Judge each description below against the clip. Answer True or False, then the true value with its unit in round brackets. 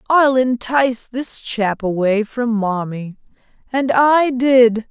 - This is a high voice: True (240 Hz)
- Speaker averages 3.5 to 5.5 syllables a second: False (3.3 syllables/s)